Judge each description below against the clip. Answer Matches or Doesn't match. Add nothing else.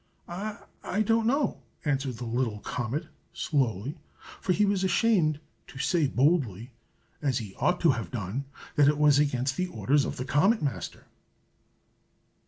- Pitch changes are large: Matches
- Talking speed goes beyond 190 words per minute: Doesn't match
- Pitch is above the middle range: Doesn't match